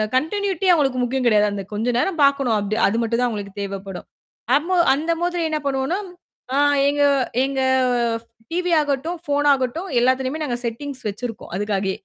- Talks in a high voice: Yes, very high, 265 Hz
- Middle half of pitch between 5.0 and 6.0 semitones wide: Yes, average, 5.3 semitones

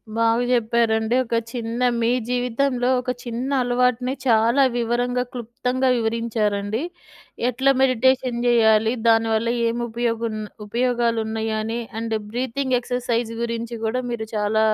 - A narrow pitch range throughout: Yes, narrow, 1.8 semitones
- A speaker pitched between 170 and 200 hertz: No, high, 235 Hz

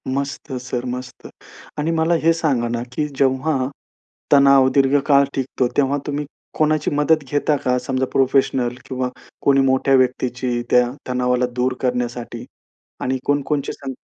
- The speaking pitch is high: No, low, 135 Hz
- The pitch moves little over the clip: Yes, narrow, 2.3 semitones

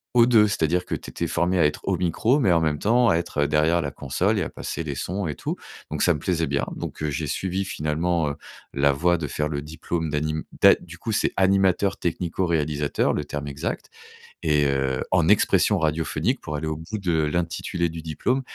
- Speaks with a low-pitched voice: Yes, very low, 80 Hz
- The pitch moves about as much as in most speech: Yes, average, 3.4 semitones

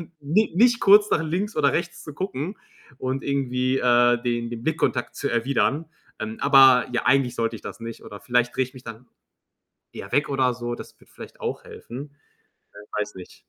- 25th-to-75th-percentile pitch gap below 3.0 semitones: No, average, 3.9 semitones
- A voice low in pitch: Yes, low, 130 Hz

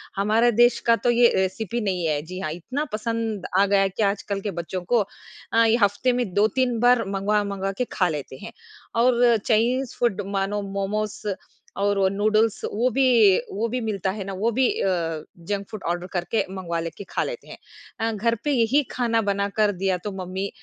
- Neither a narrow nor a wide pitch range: Yes, average, 3.1 semitones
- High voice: Yes, high, 210 Hz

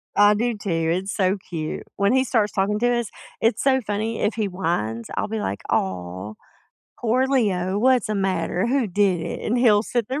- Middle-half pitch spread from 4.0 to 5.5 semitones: Yes, average, 4.6 semitones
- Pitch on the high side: Yes, high, 205 Hz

